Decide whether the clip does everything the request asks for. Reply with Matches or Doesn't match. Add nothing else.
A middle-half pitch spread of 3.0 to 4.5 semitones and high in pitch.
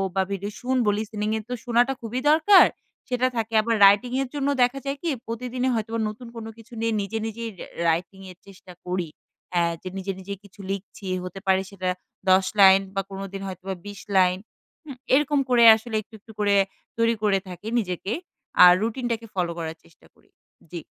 Matches